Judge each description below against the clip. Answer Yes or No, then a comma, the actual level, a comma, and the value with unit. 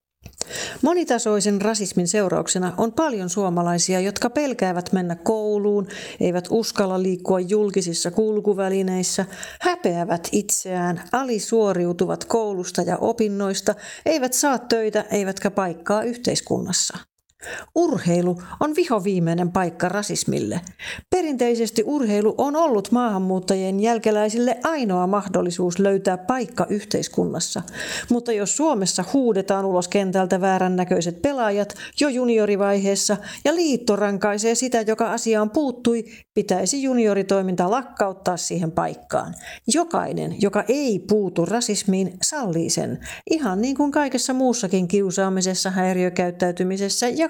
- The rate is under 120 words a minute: Yes, average, 105 wpm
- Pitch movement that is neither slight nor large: Yes, average, 3.9 semitones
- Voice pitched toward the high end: Yes, high, 205 Hz